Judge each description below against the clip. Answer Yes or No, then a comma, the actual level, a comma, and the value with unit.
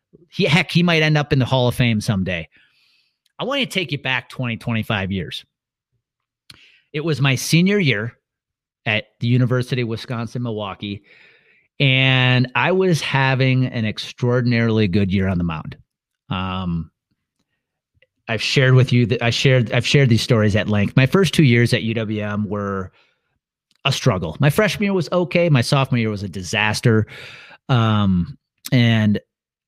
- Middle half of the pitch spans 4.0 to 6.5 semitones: Yes, average, 4.4 semitones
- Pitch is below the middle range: Yes, low, 125 Hz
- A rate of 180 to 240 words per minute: No, average, 160 wpm